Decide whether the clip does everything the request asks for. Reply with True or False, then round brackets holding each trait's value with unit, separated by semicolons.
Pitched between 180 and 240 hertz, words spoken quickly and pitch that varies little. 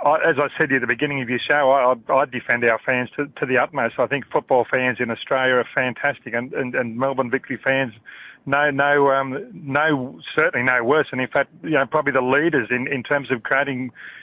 False (135 Hz; 225 wpm; 1.9 semitones)